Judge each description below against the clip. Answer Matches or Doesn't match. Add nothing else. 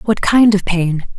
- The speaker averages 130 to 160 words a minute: Doesn't match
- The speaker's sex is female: Matches